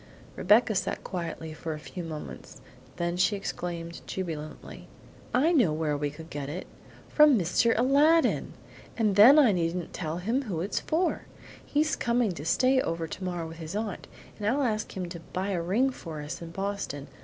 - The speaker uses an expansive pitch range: Yes, wide, 6.0 semitones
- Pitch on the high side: No, medium, 180 Hz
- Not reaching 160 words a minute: No, average, 180 wpm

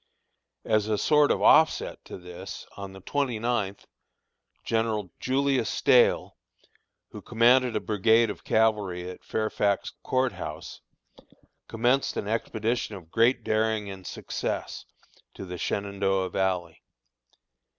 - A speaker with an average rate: No, slow, 120 wpm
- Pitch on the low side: Yes, low, 110 Hz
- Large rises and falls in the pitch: No, average, 3.7 semitones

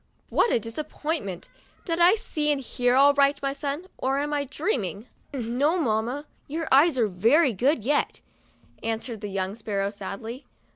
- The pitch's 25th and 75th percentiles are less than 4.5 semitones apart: No, average, 5.0 semitones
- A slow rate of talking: No, average, 165 wpm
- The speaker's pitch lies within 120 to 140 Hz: No, very high, 270 Hz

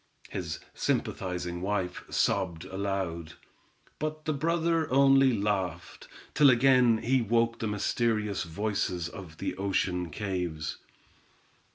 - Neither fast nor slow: No, slow, 105 wpm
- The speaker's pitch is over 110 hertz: No, low, 105 Hz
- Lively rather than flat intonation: Yes, wide, 6.1 semitones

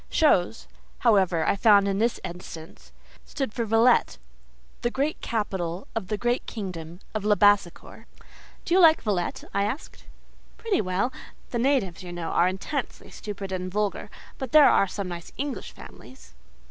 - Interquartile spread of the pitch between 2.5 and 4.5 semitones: No, average, 5.0 semitones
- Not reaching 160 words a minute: Yes, average, 150 wpm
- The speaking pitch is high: Yes, high, 200 Hz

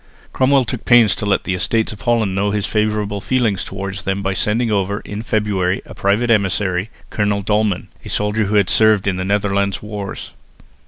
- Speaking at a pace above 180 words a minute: Yes, average, 190 wpm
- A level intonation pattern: Yes, narrow, 1.8 semitones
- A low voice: Yes, low, 105 Hz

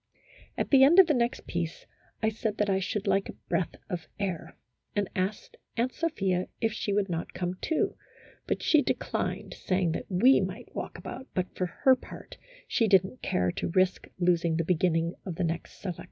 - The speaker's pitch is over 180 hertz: Yes, high, 190 Hz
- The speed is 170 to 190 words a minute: No, average, 200 wpm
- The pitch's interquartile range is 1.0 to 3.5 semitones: No, average, 4.1 semitones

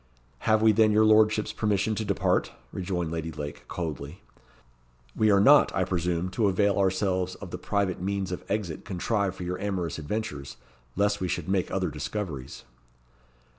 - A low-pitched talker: Yes, very low, 95 Hz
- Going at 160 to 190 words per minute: Yes, average, 165 wpm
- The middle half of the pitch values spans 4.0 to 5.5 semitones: No, average, 3.1 semitones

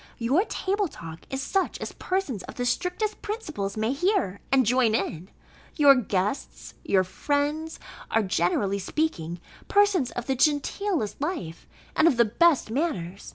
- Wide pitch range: Yes, wide, 9.0 semitones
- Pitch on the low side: No, very high, 265 Hz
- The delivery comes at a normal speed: Yes, average, 155 wpm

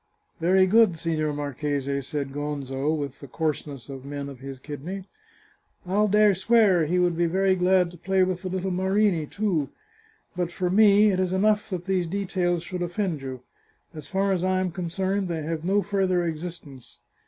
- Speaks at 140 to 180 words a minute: No, average, 190 wpm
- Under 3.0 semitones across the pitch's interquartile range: No, average, 4.2 semitones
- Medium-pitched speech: Yes, medium, 175 Hz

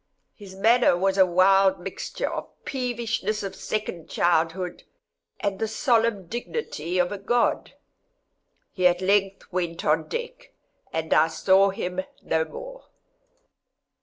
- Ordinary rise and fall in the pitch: Yes, average, 3.9 semitones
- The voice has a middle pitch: No, high, 195 Hz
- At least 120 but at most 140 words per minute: Yes, slow, 135 wpm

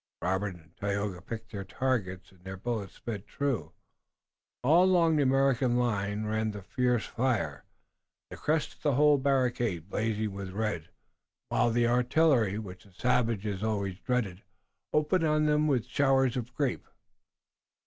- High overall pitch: No, low, 115 Hz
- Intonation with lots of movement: No, average, 4.9 semitones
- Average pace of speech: Yes, average, 150 wpm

